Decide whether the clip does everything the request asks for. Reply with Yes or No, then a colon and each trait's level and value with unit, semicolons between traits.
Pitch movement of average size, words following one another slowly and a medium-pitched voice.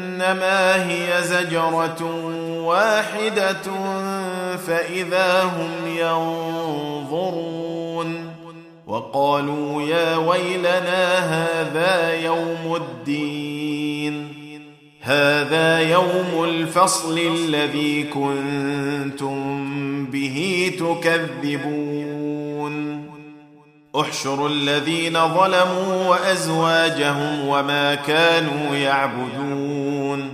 Yes: average, 3.1 semitones; slow, 55 wpm; medium, 165 Hz